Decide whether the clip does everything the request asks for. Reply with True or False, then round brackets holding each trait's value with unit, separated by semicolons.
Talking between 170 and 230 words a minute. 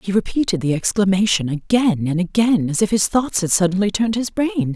True (200 wpm)